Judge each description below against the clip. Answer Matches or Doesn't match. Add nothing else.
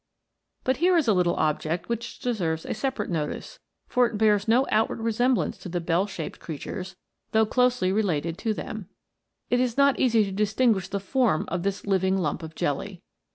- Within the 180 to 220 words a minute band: Matches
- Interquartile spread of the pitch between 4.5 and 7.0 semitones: Matches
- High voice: Matches